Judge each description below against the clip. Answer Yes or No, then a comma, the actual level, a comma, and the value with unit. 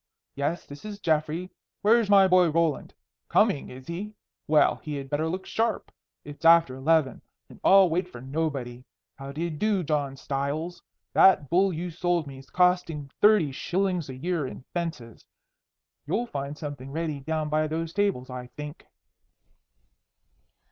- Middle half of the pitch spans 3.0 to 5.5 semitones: Yes, average, 4.2 semitones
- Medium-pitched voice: Yes, medium, 160 Hz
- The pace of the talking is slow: No, average, 155 wpm